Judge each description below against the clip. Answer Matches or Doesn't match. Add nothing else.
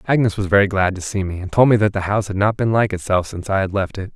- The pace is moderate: Doesn't match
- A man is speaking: Matches